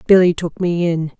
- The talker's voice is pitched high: No, medium, 170 Hz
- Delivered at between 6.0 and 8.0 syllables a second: No, 5.1 syllables/s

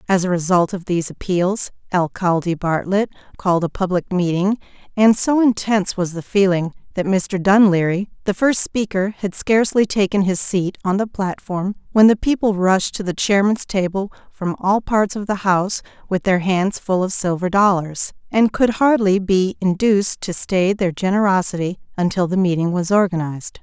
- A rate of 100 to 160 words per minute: No, average, 170 wpm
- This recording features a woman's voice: Yes, female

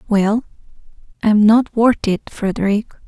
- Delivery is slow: Yes, slow, 115 wpm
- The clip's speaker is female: Yes, female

